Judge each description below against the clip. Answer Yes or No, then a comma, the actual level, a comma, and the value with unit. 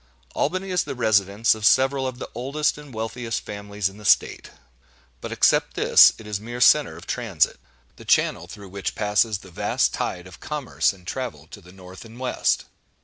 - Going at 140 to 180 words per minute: No, average, 190 wpm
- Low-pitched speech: Yes, low, 110 Hz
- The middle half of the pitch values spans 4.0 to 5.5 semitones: Yes, average, 4.5 semitones